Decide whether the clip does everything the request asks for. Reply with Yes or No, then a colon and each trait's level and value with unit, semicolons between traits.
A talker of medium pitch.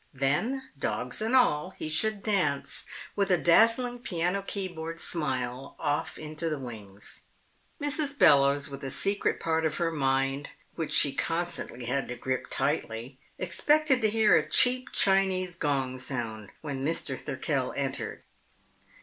Yes: medium, 160 Hz